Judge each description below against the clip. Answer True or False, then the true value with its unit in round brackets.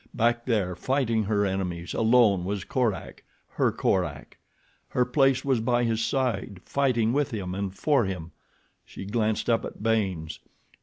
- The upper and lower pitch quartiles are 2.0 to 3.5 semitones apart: False (4.3 semitones)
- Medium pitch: False (110 Hz)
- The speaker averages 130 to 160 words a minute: True (145 wpm)